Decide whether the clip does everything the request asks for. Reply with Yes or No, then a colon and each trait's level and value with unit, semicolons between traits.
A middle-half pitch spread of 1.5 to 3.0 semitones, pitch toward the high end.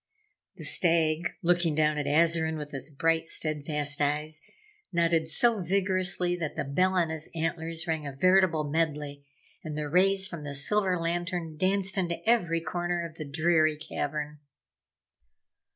No: narrow, 2.6 semitones; medium, 165 Hz